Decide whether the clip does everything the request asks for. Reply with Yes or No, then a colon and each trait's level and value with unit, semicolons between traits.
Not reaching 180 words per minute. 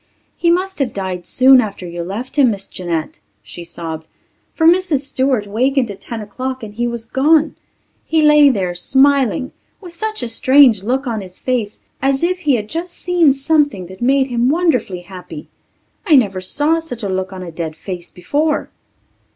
No: average, 185 wpm